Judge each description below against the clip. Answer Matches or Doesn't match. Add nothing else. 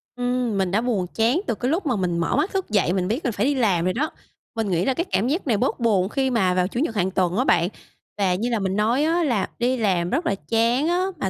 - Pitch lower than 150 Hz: Doesn't match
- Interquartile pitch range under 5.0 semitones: Doesn't match